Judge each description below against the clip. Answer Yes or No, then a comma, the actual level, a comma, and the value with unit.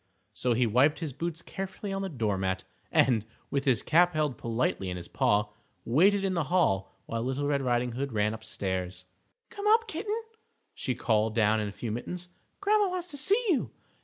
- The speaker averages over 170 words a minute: Yes, average, 190 wpm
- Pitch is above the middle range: No, low, 135 Hz